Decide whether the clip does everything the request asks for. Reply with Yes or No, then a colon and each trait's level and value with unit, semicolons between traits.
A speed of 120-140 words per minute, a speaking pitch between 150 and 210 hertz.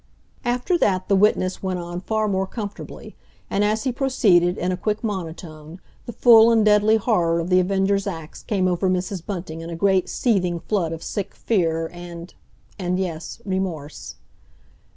No: average, 165 wpm; high, 190 Hz